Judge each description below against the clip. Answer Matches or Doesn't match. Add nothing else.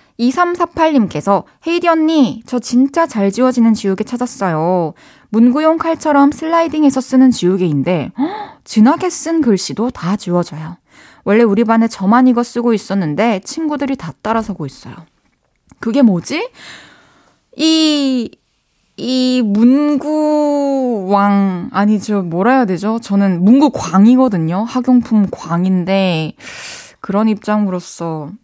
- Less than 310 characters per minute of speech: Matches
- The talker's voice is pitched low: Doesn't match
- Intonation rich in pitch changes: Matches